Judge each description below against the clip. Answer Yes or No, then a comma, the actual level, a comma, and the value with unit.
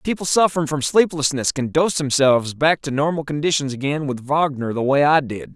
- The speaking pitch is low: No, medium, 145 Hz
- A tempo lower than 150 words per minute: No, average, 195 wpm